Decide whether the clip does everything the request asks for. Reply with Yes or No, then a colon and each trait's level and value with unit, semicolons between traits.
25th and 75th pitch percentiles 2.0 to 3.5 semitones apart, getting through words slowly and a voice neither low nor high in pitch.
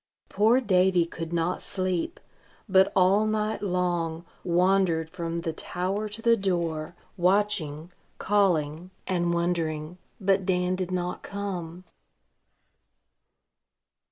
Yes: narrow, 2.5 semitones; slow, 105 wpm; medium, 180 Hz